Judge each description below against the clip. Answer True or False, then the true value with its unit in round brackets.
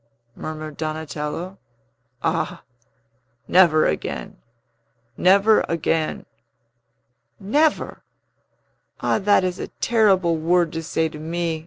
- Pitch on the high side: False (170 Hz)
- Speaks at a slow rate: True (95 wpm)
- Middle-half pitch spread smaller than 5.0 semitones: True (3.2 semitones)